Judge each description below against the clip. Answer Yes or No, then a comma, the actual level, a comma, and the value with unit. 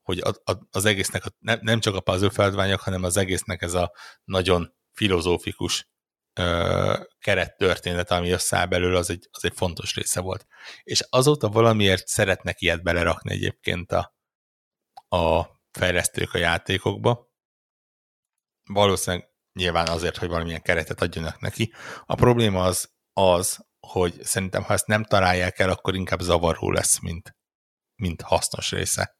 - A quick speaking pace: No, average, 130 wpm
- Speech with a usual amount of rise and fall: Yes, average, 3.1 semitones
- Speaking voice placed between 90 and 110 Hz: Yes, very low, 95 Hz